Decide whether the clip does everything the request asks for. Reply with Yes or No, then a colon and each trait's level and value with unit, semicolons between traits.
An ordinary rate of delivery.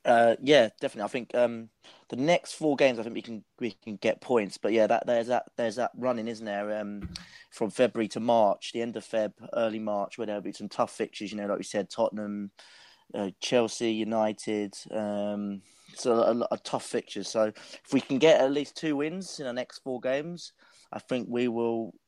No: fast, 220 wpm